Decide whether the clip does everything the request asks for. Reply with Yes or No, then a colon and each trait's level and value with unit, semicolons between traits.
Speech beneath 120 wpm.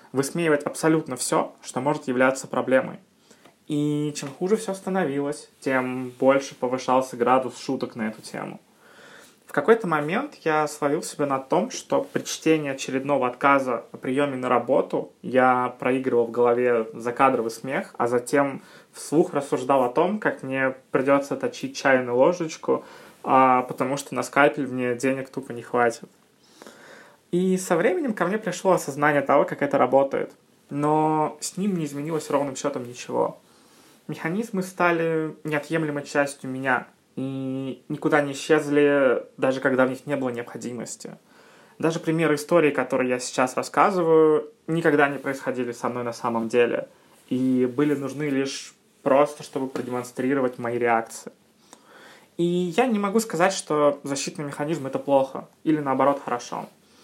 No: average, 145 wpm